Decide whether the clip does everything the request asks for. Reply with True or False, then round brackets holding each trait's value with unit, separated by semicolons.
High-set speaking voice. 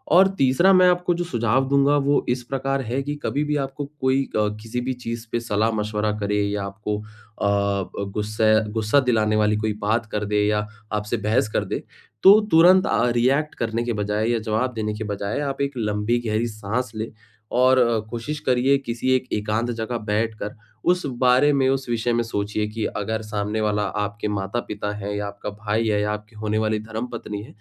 False (110 Hz)